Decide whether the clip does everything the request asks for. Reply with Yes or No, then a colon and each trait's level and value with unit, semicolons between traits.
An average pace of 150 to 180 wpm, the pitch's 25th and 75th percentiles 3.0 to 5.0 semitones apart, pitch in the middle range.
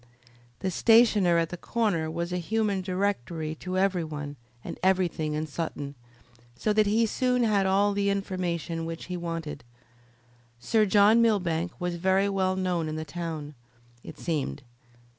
Yes: average, 155 wpm; average, 3.5 semitones; medium, 180 Hz